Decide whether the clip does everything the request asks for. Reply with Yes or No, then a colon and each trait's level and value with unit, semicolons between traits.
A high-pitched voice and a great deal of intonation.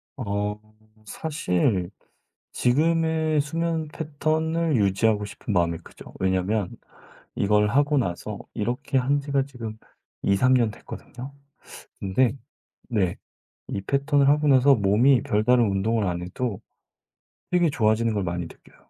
No: low, 120 Hz; wide, 5.8 semitones